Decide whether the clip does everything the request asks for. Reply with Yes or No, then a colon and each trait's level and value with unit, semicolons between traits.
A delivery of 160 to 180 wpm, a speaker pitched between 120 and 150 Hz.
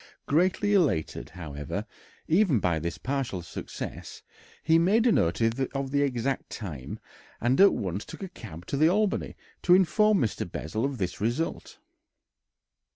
No: average, 150 wpm; low, 135 Hz